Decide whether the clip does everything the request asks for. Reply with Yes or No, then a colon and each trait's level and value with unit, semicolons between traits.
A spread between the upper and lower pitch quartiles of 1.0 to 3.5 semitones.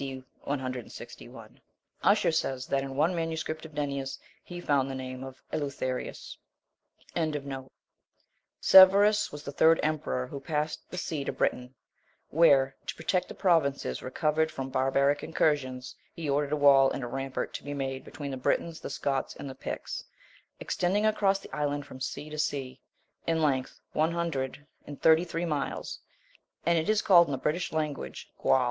Yes: average, 3.2 semitones